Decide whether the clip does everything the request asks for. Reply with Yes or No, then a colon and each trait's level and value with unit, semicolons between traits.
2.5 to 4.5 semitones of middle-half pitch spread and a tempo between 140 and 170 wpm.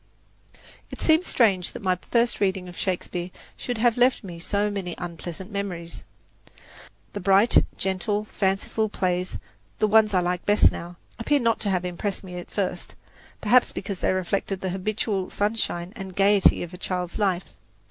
Yes: average, 2.8 semitones; average, 165 wpm